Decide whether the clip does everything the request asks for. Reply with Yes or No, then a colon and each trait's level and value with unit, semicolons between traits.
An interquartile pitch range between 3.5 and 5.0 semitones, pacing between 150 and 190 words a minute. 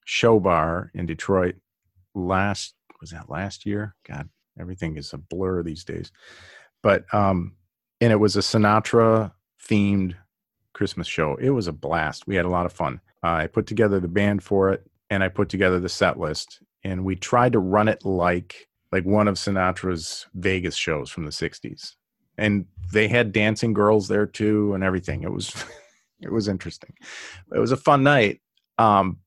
No: average, 2.9 semitones; average, 180 wpm